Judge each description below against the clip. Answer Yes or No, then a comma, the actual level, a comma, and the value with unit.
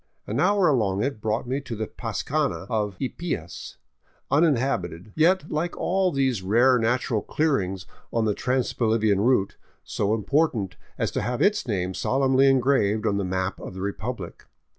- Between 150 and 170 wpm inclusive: Yes, average, 160 wpm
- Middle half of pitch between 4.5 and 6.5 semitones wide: Yes, wide, 5.4 semitones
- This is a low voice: Yes, low, 120 Hz